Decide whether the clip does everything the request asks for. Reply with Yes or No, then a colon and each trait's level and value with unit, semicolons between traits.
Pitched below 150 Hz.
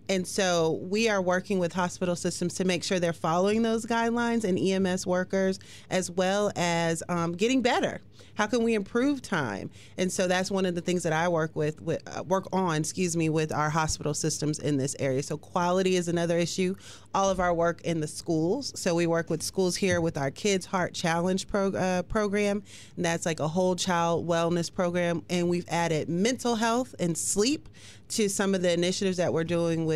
No: medium, 180 Hz